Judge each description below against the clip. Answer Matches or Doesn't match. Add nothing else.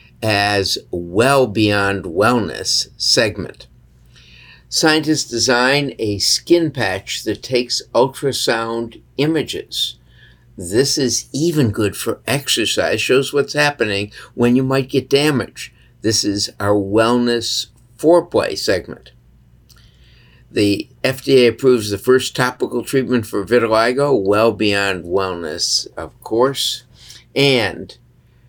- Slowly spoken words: Matches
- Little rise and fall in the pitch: Doesn't match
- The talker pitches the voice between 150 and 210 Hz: Doesn't match